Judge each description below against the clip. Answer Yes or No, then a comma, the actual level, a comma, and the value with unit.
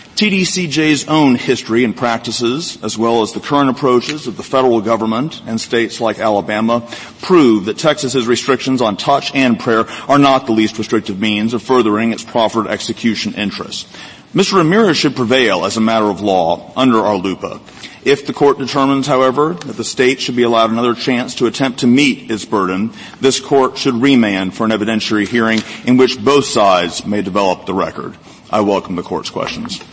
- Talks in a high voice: No, low, 125 Hz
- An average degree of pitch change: Yes, average, 3.6 semitones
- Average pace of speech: Yes, average, 180 wpm